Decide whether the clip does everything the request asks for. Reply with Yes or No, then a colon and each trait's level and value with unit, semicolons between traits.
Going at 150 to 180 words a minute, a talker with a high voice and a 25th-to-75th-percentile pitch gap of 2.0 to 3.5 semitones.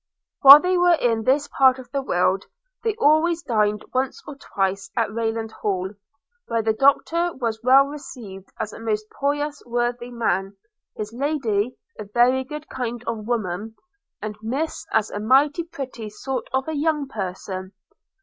No: average, 160 wpm; high, 240 Hz; average, 4.8 semitones